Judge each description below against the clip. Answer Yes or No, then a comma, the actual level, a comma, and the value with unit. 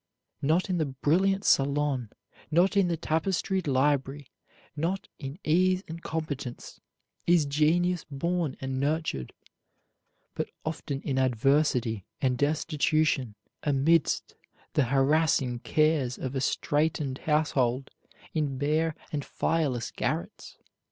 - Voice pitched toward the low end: No, medium, 150 Hz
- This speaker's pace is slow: Yes, slow, 110 wpm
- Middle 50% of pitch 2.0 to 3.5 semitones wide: Yes, average, 3.2 semitones